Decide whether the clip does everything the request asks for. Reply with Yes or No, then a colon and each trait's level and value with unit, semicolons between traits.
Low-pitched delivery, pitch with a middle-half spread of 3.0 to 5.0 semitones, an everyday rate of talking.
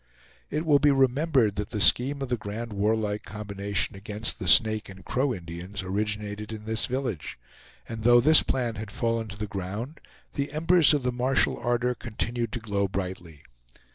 Yes: low, 110 Hz; average, 3.7 semitones; average, 175 wpm